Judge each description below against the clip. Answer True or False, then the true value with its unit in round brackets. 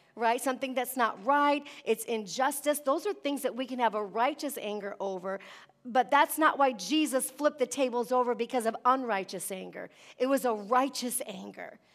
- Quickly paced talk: False (180 wpm)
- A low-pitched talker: False (255 Hz)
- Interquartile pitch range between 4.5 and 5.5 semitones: False (3.5 semitones)